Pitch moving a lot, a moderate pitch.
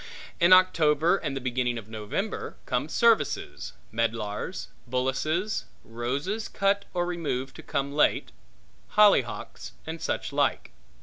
Yes: wide, 7.1 semitones; medium, 150 Hz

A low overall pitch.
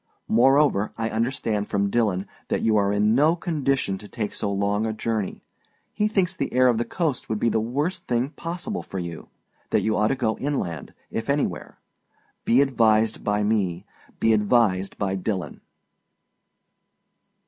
Yes: low, 110 Hz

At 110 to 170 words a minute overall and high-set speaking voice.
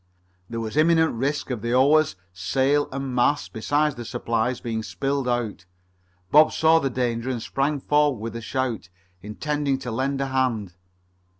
No: average, 165 wpm; low, 130 Hz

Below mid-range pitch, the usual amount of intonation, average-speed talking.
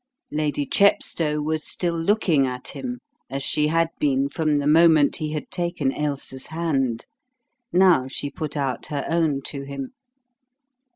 No: medium, 150 Hz; average, 3.1 semitones; average, 150 wpm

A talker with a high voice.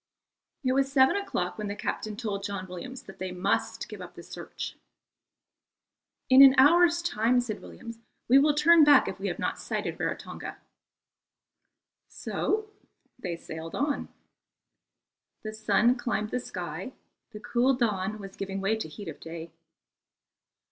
Yes: high, 220 Hz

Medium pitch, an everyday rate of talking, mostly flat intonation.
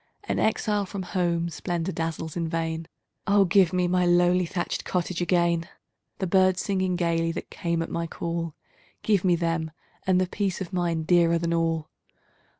Yes: medium, 175 Hz; average, 170 wpm; narrow, 1.8 semitones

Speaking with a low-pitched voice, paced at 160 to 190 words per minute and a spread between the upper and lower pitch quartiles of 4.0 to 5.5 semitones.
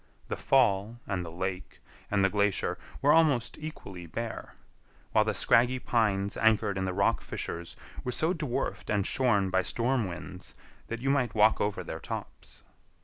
Yes: low, 105 Hz; average, 165 wpm; average, 4.3 semitones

